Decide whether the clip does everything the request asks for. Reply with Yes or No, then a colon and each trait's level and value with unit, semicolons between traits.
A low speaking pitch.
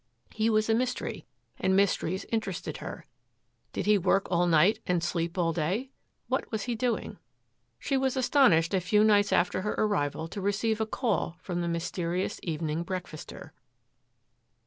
No: high, 190 Hz